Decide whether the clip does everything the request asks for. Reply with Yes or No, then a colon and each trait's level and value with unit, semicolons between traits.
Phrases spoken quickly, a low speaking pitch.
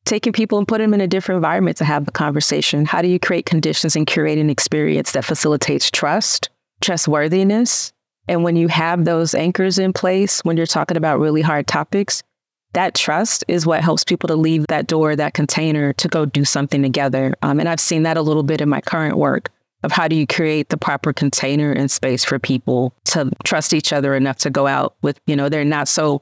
No: fast, 220 wpm; medium, 155 Hz